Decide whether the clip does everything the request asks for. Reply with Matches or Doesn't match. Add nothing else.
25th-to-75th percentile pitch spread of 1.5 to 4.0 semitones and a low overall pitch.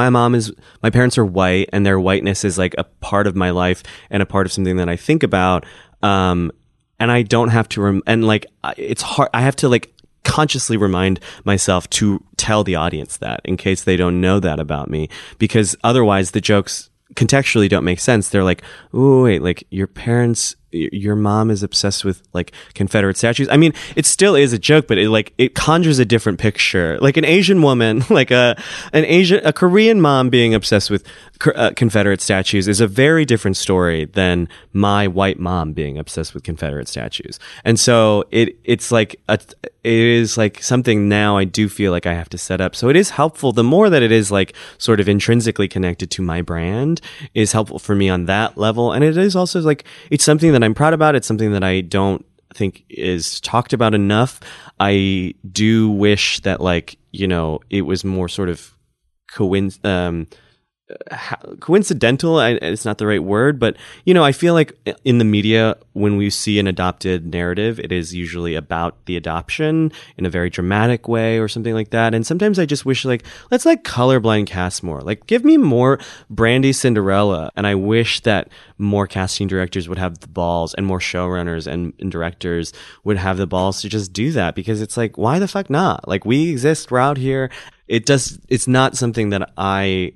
Doesn't match